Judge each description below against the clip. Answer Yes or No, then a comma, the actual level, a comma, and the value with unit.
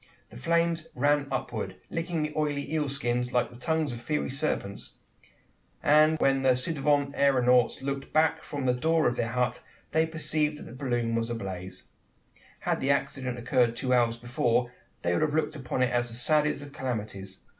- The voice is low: Yes, low, 130 Hz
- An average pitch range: Yes, average, 3.9 semitones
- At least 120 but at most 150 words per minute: No, average, 185 wpm